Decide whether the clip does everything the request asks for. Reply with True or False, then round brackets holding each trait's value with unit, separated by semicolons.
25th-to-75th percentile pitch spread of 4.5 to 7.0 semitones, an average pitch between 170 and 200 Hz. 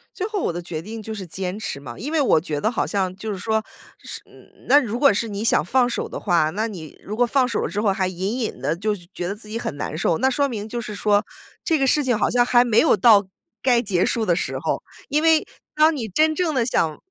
False (4.9 semitones; 220 Hz)